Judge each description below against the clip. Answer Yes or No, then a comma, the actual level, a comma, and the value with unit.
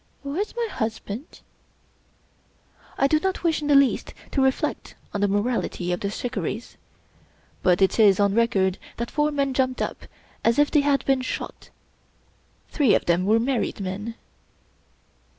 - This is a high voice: Yes, high, 240 Hz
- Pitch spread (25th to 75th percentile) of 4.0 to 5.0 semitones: No, wide, 5.6 semitones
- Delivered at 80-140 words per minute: No, average, 165 wpm